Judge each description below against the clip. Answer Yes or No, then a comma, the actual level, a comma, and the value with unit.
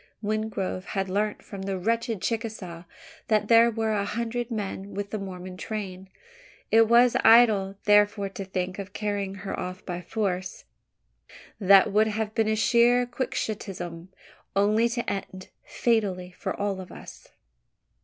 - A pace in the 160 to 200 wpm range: No, average, 145 wpm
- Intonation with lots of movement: No, average, 2.7 semitones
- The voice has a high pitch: Yes, high, 205 Hz